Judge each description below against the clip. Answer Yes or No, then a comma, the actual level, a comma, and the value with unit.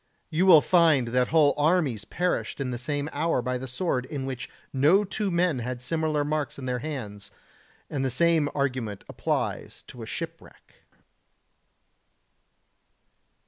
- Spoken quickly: No, average, 145 wpm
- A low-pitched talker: No, medium, 145 Hz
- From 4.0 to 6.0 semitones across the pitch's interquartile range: Yes, average, 4.3 semitones